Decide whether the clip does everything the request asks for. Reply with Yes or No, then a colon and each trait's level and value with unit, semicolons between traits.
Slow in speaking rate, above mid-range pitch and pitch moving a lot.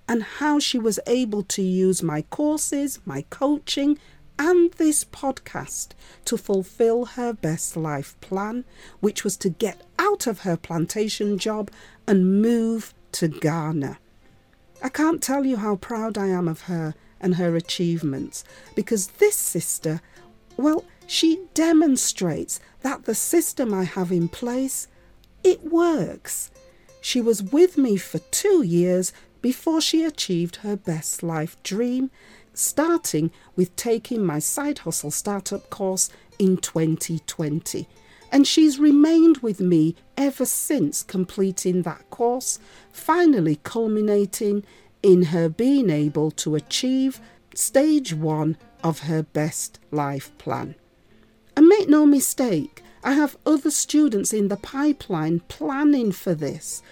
Yes: slow, 130 wpm; high, 205 Hz; wide, 8.6 semitones